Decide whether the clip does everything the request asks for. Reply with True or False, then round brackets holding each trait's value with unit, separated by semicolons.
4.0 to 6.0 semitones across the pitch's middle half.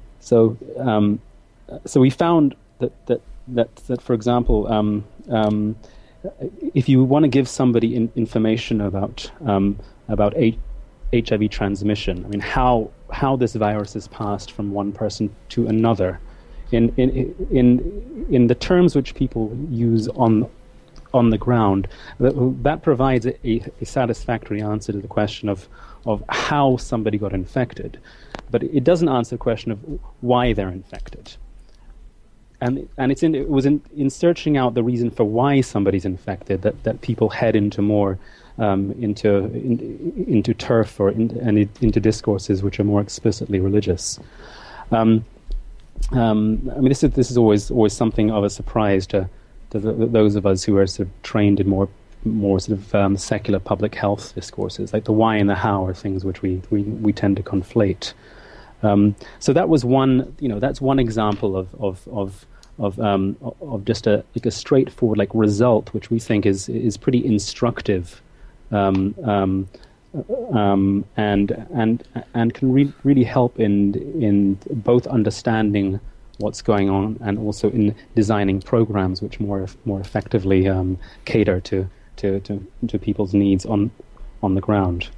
False (3.2 semitones)